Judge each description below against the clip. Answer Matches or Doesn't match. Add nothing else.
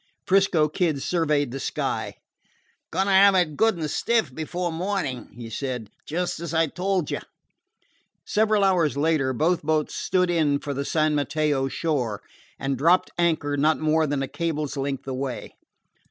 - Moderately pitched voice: Matches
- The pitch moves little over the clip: Doesn't match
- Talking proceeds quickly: Doesn't match